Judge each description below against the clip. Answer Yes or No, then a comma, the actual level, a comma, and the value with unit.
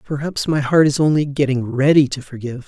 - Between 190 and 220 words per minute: Yes, average, 200 wpm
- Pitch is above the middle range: No, medium, 140 Hz